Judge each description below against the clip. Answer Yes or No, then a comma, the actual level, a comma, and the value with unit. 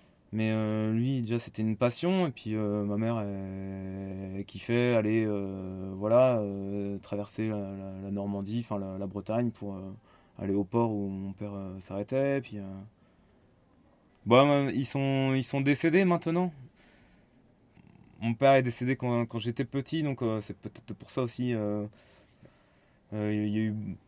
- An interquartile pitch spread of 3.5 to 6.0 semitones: Yes, average, 3.9 semitones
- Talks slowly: No, average, 170 wpm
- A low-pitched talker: Yes, low, 110 Hz